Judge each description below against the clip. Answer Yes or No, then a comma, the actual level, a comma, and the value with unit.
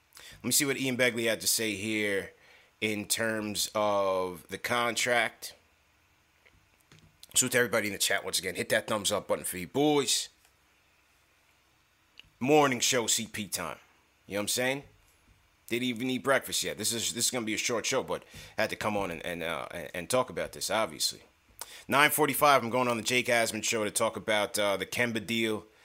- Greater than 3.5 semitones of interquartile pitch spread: Yes, average, 3.9 semitones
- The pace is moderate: Yes, average, 195 wpm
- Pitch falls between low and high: No, low, 115 Hz